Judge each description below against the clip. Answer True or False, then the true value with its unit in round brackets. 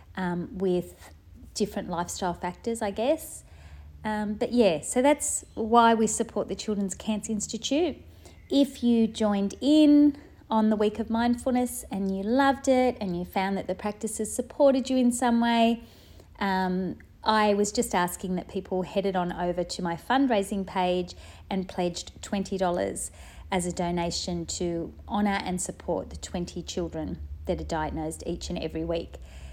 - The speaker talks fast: False (155 wpm)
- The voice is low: False (200 Hz)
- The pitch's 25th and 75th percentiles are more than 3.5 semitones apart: True (4.6 semitones)